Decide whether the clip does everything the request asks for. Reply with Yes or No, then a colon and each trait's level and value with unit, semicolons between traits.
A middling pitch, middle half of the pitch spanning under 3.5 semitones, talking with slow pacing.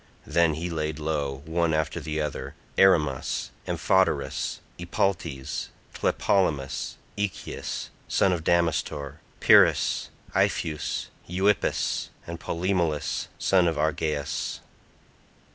No: very low, 80 Hz; narrow, 2.6 semitones; slow, 95 wpm